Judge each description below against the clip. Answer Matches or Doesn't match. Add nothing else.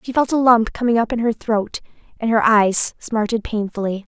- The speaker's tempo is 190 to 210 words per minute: Matches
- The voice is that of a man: Doesn't match